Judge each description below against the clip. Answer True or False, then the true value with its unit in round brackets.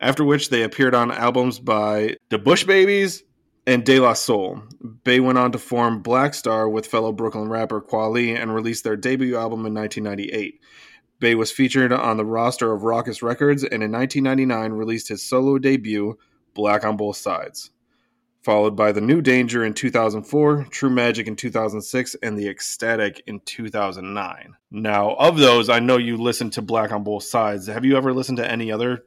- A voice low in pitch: True (115 Hz)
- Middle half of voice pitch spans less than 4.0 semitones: True (2.9 semitones)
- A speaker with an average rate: True (180 wpm)